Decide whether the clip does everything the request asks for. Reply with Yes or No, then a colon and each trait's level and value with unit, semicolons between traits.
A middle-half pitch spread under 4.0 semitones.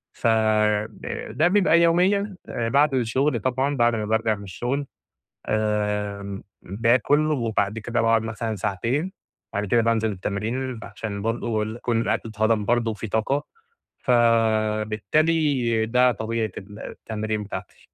Yes: average, 2.8 semitones